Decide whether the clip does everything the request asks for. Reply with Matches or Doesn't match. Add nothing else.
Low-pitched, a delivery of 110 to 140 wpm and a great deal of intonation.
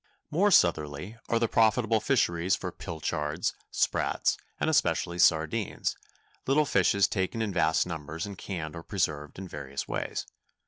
Matches